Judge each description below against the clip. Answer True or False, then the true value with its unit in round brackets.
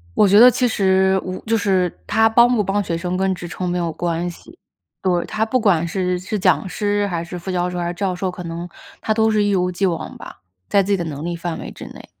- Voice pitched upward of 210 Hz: False (185 Hz)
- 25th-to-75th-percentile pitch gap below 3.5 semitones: True (2.6 semitones)